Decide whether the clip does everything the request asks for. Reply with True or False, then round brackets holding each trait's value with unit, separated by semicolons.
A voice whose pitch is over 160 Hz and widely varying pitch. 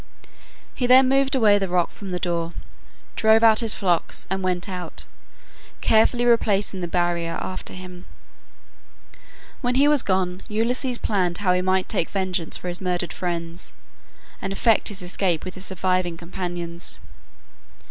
False (185 Hz; 3.7 semitones)